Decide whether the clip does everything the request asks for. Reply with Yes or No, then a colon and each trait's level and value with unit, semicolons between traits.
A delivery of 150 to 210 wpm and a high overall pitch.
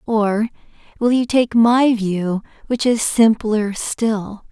No: slow, 135 wpm; high, 220 Hz